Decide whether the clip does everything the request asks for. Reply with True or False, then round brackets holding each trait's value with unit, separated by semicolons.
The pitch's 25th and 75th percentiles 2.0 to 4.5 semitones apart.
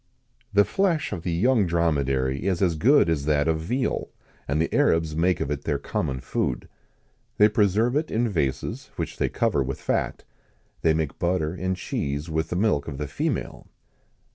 False (5.6 semitones)